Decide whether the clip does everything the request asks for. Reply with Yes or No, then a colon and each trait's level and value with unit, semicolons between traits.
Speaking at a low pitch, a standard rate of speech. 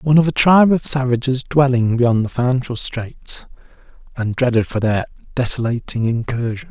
Yes: low, 125 Hz; average, 150 wpm